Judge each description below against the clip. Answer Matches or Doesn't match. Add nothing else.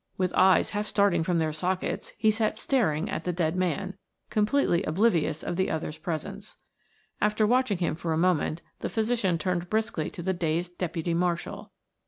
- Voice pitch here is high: Doesn't match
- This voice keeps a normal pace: Matches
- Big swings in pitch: Doesn't match